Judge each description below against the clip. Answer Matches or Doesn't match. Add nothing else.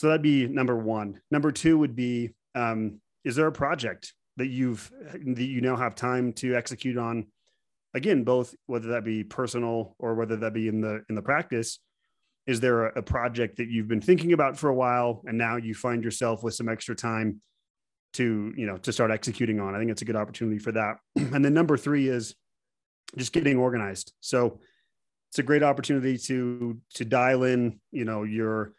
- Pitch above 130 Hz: Doesn't match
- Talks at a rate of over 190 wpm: Matches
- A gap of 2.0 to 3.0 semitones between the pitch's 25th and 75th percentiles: Matches